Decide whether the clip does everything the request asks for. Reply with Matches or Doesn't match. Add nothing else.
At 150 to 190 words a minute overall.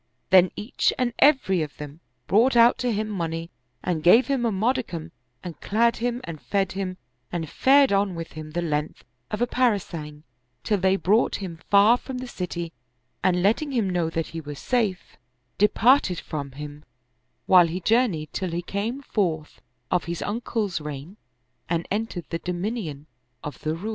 Matches